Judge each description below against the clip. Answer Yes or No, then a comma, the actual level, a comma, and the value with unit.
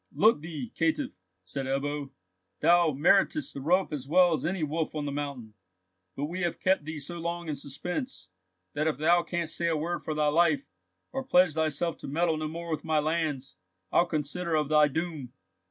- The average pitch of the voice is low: No, medium, 160 Hz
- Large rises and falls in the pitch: No, average, 2.9 semitones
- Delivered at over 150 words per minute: Yes, average, 195 wpm